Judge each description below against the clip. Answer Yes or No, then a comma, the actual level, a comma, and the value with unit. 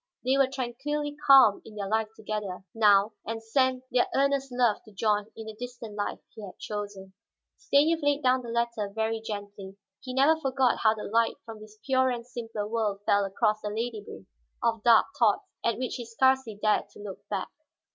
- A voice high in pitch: Yes, high, 225 Hz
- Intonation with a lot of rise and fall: No, average, 3.7 semitones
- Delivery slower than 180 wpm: No, average, 185 wpm